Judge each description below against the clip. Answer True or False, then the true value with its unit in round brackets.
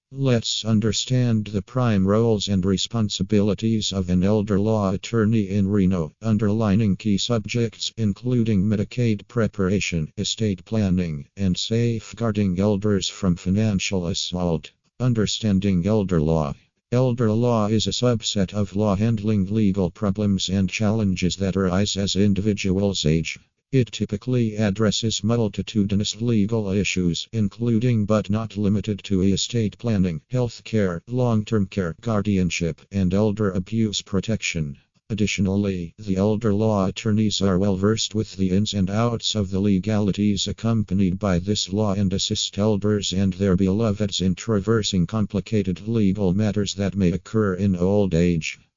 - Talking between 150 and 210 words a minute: False (135 wpm)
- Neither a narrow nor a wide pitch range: False (2.3 semitones)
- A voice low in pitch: True (100 Hz)